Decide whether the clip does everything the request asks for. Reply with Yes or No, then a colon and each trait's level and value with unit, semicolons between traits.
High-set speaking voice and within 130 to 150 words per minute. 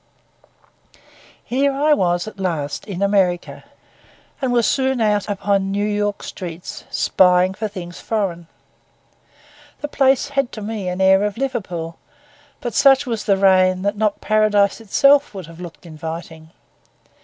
Yes: high, 200 Hz; average, 145 wpm